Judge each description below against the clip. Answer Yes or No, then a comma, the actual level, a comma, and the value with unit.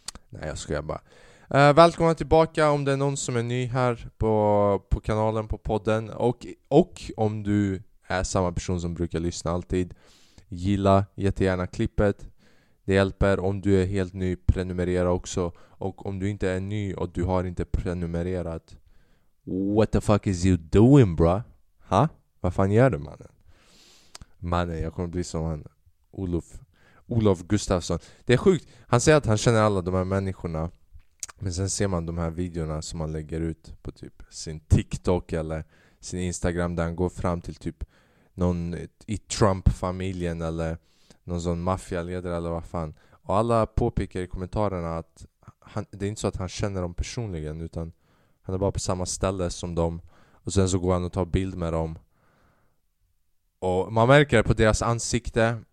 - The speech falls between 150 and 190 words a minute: Yes, average, 175 wpm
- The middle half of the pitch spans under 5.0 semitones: Yes, average, 3.5 semitones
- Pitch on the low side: Yes, very low, 95 Hz